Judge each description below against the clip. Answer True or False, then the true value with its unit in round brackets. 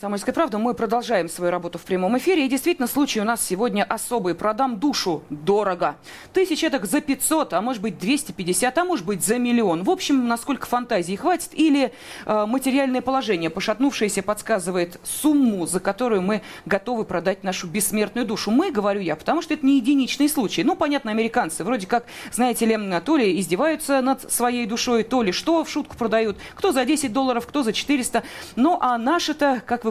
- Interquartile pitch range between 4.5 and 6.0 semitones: True (4.9 semitones)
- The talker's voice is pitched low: False (240 Hz)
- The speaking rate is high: True (185 wpm)